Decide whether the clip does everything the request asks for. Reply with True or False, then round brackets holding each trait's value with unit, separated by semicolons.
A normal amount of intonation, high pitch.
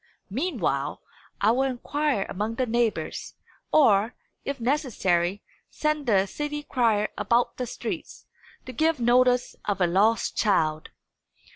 True (5.0 semitones; 235 Hz)